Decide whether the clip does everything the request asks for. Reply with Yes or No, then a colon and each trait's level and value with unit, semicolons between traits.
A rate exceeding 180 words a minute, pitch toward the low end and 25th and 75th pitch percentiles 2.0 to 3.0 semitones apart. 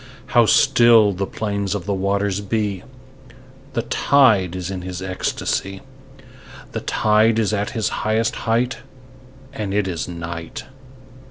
No: slow, 135 wpm; low, 100 Hz; average, 2.7 semitones